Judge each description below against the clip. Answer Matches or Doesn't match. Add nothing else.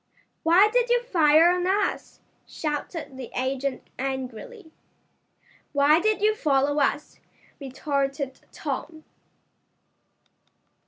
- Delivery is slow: Matches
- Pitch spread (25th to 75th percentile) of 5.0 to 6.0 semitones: Matches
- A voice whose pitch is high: Matches